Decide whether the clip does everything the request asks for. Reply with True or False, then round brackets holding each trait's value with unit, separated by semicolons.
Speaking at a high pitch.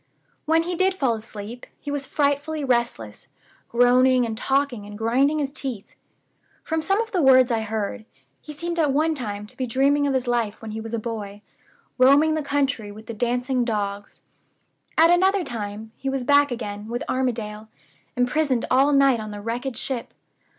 True (250 Hz)